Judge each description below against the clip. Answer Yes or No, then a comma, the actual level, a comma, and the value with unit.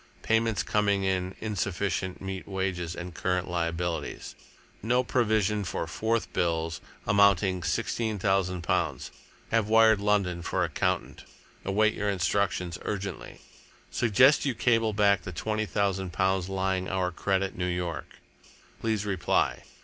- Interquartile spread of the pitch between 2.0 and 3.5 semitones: Yes, average, 2.9 semitones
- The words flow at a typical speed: No, slow, 125 wpm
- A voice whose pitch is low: Yes, very low, 95 Hz